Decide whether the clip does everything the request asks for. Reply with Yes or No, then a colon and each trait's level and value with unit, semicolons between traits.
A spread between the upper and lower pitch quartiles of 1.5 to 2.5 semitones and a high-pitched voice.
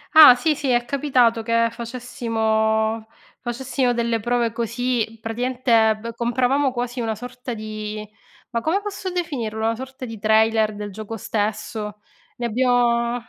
Yes: narrow, 2.2 semitones; high, 235 Hz